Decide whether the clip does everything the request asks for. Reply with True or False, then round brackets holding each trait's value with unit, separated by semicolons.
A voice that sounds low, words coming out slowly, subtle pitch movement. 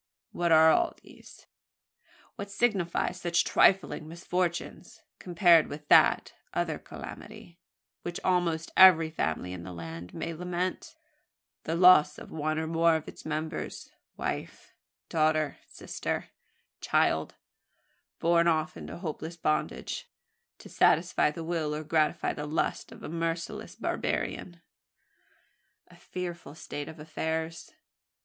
False (165 Hz; 125 wpm; 2.0 semitones)